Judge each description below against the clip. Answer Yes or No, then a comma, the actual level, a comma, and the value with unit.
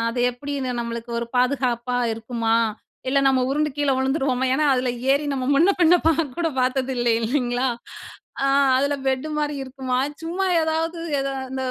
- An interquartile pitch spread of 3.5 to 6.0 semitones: No, average, 2.8 semitones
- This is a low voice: No, very high, 265 Hz